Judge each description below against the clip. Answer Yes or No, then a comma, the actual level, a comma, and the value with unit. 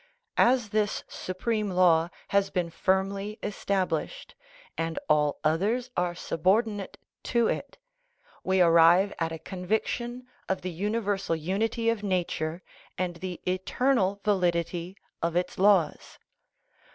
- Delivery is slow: Yes, slow, 120 wpm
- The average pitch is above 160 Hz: Yes, high, 190 Hz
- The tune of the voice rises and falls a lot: No, average, 3.3 semitones